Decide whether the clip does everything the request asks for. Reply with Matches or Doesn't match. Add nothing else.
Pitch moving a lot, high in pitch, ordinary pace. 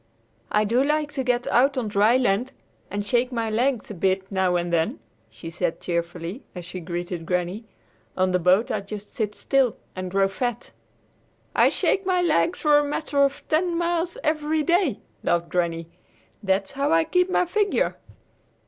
Matches